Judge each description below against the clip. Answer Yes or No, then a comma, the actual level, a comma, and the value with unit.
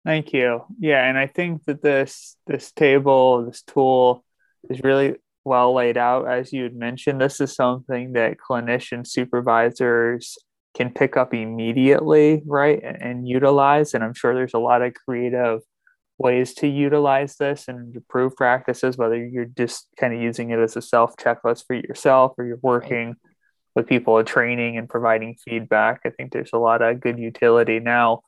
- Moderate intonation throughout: No, narrow, 2.3 semitones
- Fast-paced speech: No, average, 170 wpm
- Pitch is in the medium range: No, low, 125 Hz